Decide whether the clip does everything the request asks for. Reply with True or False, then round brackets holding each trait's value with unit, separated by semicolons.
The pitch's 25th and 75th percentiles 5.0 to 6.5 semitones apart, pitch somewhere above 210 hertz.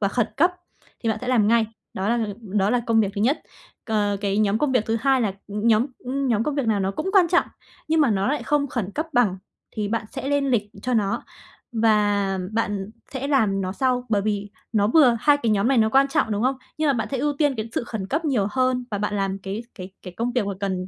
False (4.4 semitones; 225 Hz)